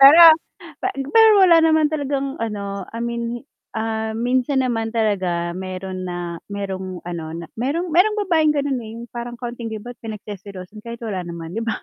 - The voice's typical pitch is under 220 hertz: No, high, 225 Hz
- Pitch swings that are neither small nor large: No, wide, 6.0 semitones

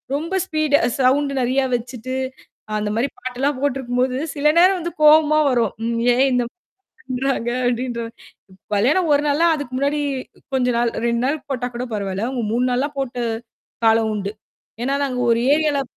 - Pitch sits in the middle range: No, very high, 255 Hz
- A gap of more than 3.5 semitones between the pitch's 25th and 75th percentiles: No, average, 3.2 semitones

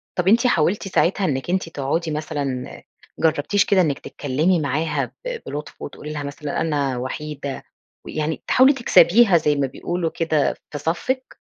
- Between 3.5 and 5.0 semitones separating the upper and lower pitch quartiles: Yes, average, 4.0 semitones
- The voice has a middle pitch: Yes, medium, 155 Hz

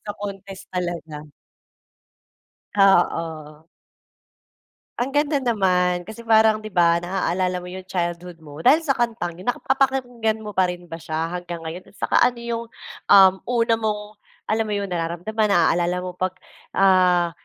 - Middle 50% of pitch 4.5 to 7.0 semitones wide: No, average, 4.0 semitones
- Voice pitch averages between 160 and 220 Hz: Yes, high, 190 Hz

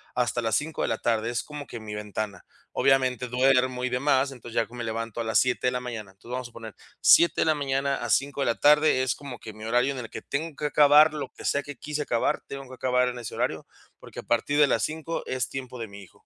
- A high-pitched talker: No, low, 125 Hz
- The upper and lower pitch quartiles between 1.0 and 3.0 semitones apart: No, average, 3.4 semitones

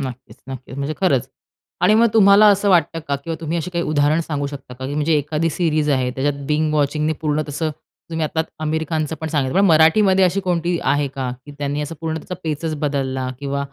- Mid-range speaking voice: Yes, medium, 155 Hz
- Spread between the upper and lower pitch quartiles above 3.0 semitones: No, average, 2.7 semitones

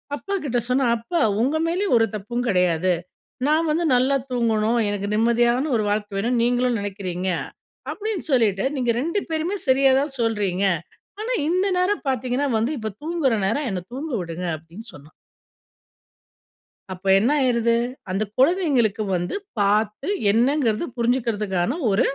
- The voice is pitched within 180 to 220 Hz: No, high, 235 Hz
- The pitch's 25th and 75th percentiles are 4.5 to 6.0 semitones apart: Yes, wide, 5.4 semitones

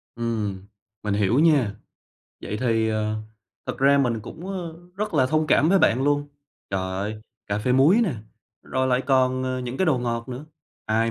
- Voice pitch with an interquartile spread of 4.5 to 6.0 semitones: Yes, average, 4.9 semitones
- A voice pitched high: No, low, 125 Hz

